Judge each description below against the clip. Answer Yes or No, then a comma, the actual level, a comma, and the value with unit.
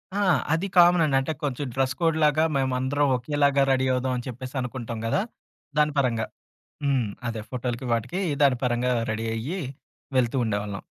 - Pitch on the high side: No, low, 130 Hz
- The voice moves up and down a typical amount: Yes, average, 3.2 semitones